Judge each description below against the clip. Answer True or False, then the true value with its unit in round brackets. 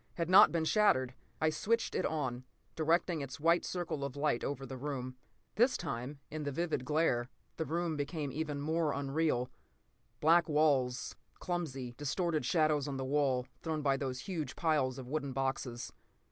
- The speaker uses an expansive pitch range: False (3.5 semitones)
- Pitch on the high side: False (150 Hz)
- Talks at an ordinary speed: True (165 wpm)